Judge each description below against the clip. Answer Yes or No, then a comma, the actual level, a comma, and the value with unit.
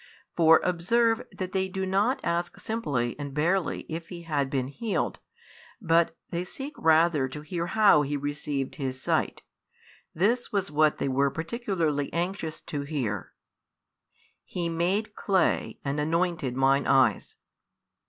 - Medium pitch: Yes, medium, 165 Hz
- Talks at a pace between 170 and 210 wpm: No, average, 140 wpm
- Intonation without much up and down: No, average, 4.8 semitones